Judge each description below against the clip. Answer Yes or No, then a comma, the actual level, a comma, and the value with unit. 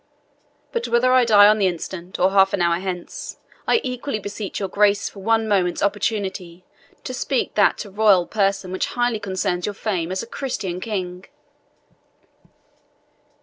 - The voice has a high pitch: Yes, high, 200 Hz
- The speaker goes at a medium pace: Yes, average, 165 wpm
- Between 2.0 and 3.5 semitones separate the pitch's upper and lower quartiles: Yes, average, 2.9 semitones